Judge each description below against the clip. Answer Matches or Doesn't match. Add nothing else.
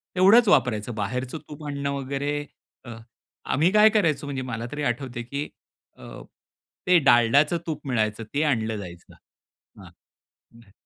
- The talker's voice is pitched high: Doesn't match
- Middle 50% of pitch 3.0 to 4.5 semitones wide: Matches